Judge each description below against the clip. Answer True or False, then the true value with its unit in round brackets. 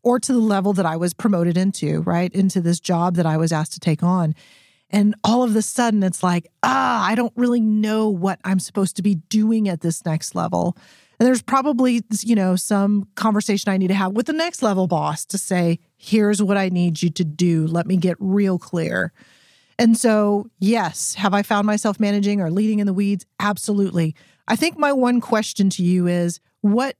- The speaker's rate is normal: False (210 wpm)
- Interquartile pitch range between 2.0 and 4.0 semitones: True (3.6 semitones)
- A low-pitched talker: False (200 Hz)